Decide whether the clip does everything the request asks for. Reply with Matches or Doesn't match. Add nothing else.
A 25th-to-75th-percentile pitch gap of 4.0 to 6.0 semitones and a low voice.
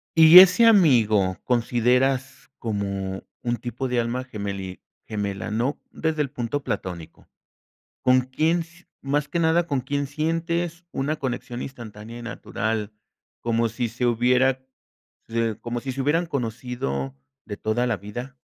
Matches